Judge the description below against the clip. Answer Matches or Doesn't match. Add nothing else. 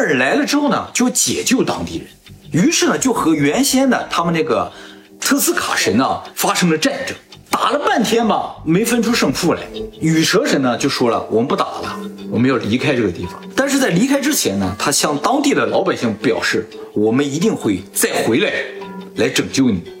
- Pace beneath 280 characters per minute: Doesn't match